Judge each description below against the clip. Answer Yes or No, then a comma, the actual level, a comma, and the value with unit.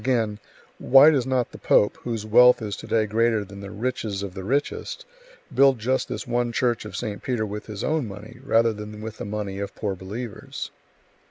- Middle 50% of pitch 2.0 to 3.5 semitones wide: Yes, average, 3.0 semitones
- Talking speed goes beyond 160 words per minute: Yes, average, 200 wpm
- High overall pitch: No, low, 110 Hz